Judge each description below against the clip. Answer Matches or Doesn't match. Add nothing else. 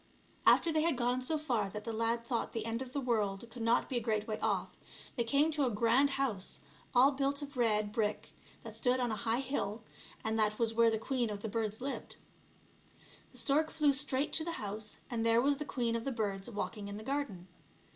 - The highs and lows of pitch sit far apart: Doesn't match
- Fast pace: Matches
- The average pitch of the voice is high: Matches